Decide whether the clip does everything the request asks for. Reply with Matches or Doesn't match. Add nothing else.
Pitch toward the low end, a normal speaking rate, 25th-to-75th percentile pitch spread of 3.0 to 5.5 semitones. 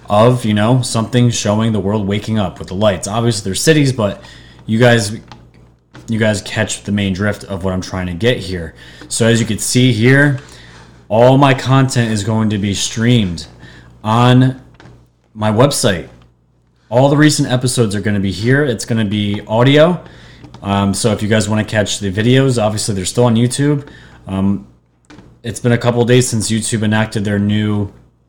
Matches